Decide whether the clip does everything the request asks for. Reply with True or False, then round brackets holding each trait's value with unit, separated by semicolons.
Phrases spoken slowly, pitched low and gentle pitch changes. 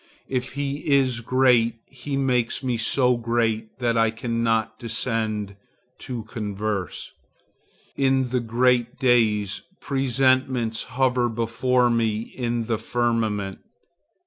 True (110 wpm; 120 Hz; 2.3 semitones)